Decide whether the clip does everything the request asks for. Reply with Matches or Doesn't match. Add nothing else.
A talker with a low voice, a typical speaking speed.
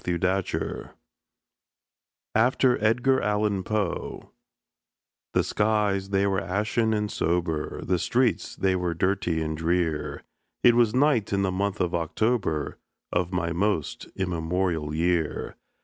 Doesn't match